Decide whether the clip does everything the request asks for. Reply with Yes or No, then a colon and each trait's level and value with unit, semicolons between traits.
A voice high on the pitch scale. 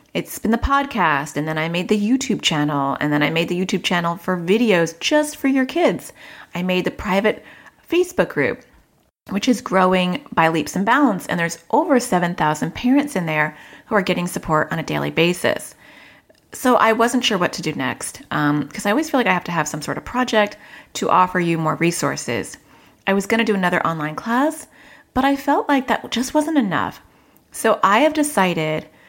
Yes: high, 195 Hz